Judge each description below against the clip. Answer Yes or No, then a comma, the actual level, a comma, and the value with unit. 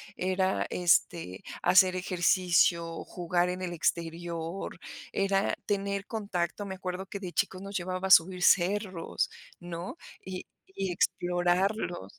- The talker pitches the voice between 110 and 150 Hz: No, medium, 180 Hz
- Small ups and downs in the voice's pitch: Yes, narrow, 1.8 semitones